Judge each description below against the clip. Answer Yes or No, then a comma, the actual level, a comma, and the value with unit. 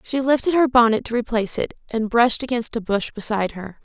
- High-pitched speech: Yes, high, 235 Hz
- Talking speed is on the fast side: Yes, fast, 220 wpm